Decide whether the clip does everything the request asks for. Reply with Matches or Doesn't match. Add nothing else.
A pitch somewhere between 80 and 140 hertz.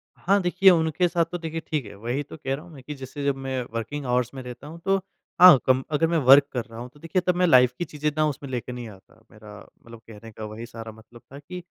Matches